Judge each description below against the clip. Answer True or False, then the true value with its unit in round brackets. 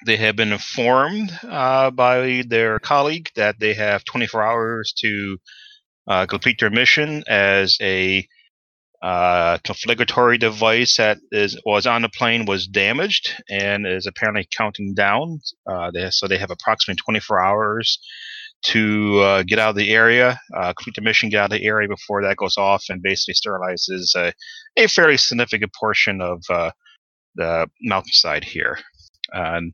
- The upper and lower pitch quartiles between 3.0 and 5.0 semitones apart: True (4.0 semitones)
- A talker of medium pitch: False (110 Hz)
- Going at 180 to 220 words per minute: False (155 wpm)